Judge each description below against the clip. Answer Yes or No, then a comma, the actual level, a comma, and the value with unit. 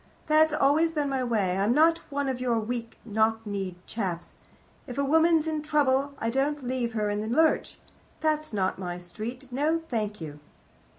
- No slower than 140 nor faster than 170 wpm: No, average, 180 wpm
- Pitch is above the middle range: Yes, very high, 255 Hz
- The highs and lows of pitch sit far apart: Yes, wide, 5.8 semitones